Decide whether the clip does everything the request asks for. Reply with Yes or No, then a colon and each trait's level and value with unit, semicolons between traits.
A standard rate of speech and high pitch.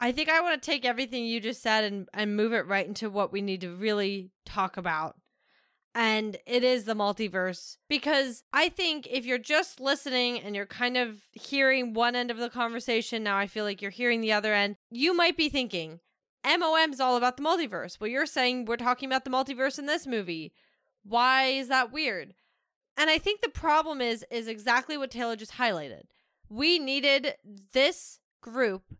Yes: average, 195 wpm; high, 245 Hz